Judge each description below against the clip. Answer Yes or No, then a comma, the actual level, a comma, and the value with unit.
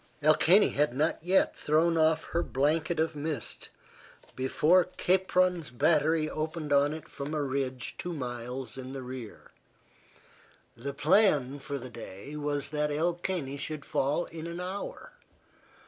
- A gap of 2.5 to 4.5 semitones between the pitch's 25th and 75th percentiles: Yes, average, 3.4 semitones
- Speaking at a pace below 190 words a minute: Yes, average, 145 wpm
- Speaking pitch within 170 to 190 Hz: No, medium, 150 Hz